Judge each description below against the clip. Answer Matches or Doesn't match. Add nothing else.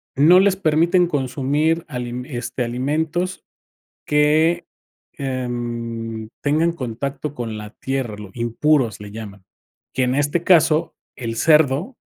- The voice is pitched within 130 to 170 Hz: Matches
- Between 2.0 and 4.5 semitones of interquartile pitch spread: Doesn't match